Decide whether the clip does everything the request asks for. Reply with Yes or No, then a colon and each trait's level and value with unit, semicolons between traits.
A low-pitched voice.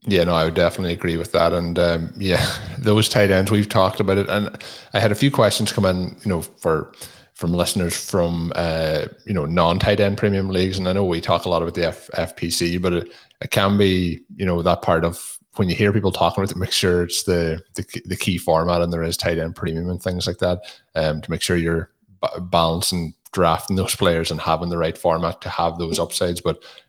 Yes: very low, 90 Hz